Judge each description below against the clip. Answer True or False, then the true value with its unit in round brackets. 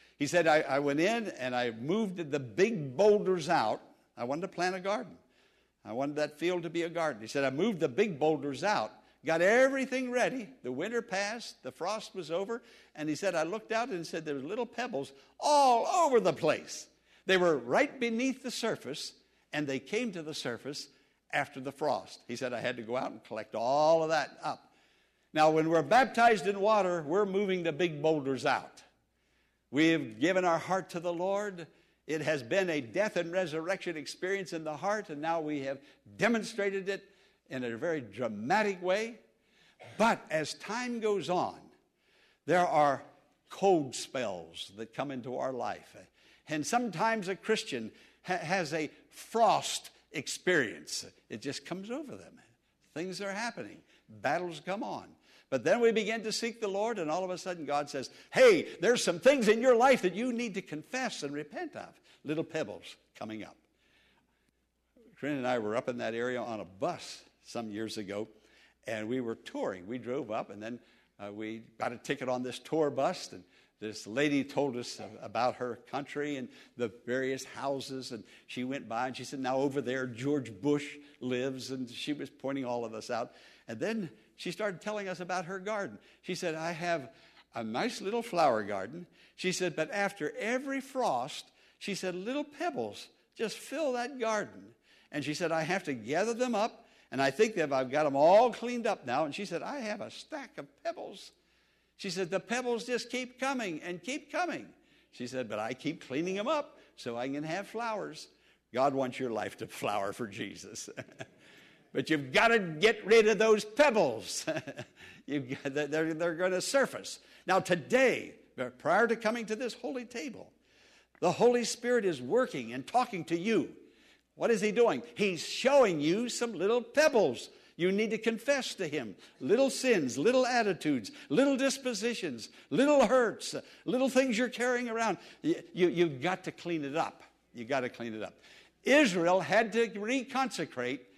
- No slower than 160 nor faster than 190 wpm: True (185 wpm)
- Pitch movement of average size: False (8.2 semitones)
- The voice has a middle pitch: True (180 Hz)